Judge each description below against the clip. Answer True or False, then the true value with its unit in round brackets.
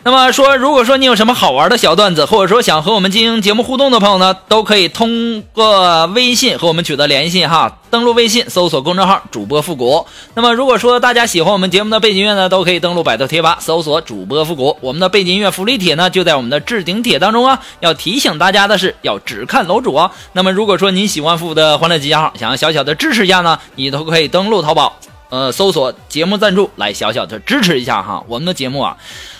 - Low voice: False (190 Hz)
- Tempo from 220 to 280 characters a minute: False (375 characters per minute)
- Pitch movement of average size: False (5.7 semitones)